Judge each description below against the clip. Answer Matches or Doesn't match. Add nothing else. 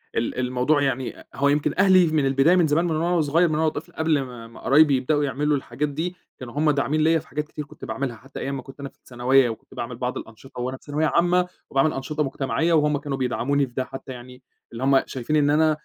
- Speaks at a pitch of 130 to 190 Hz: Matches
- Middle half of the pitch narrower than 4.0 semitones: Matches